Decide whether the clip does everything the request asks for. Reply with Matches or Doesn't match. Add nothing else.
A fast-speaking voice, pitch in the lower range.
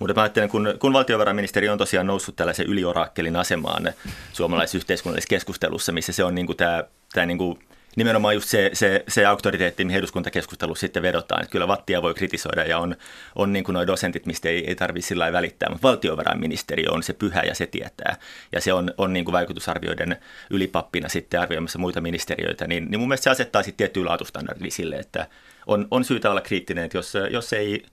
Matches